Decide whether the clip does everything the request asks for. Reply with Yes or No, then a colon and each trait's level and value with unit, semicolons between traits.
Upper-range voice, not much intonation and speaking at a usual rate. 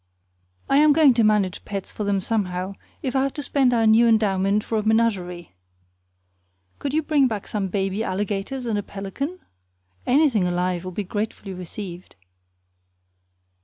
No: high, 210 Hz; average, 4.5 semitones; average, 160 wpm